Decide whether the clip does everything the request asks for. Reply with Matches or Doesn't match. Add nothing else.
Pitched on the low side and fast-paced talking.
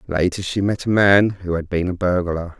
Matches